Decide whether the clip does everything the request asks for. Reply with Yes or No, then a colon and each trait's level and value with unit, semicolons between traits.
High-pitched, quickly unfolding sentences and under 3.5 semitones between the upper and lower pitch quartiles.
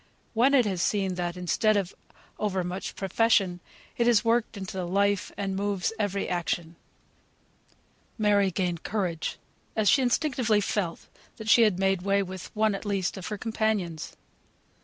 No: high, 200 Hz; average, 155 wpm; average, 2.9 semitones